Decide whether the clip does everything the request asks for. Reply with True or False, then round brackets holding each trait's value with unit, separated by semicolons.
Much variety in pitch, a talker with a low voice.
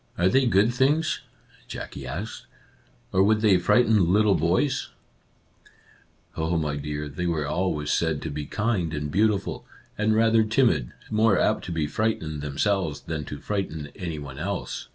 True (6.2 semitones; 90 Hz)